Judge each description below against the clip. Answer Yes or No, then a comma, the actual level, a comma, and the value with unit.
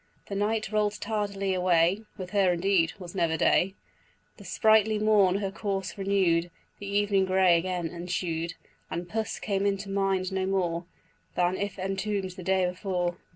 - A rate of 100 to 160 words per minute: Yes, average, 155 wpm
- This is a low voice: No, high, 190 Hz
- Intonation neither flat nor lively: No, narrow, 2.1 semitones